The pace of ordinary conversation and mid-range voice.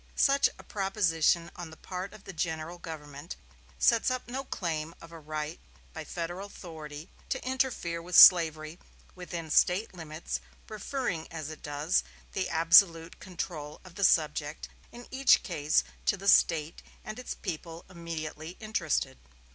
Yes: average, 145 wpm; medium, 170 Hz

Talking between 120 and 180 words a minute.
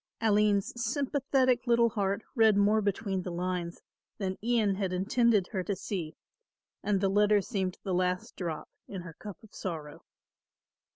Yes: average, 155 wpm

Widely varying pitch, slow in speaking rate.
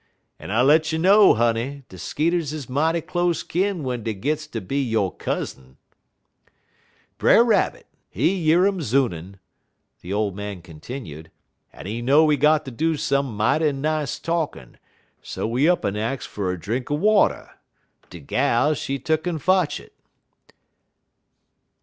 No: wide, 6.5 semitones; average, 150 wpm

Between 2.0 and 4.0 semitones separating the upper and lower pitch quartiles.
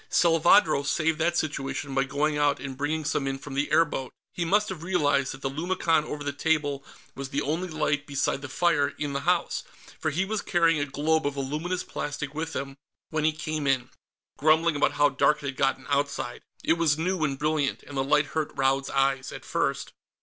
Yes: narrow, 2.5 semitones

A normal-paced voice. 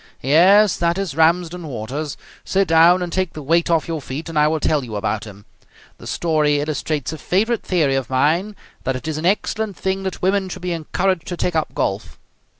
No: fast, 210 wpm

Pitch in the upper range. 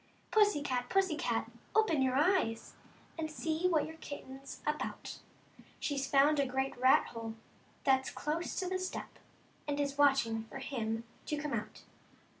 Yes: very high, 285 Hz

